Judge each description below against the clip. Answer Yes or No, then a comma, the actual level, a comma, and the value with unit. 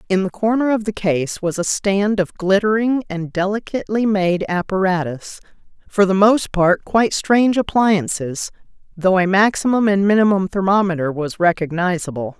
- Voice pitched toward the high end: Yes, high, 195 Hz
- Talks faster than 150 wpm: No, average, 145 wpm